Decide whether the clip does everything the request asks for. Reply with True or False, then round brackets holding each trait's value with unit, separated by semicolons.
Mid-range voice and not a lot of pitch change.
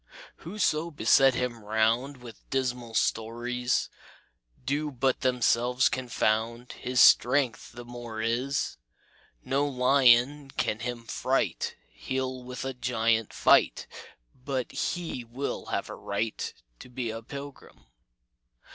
False (125 Hz; 2.3 semitones)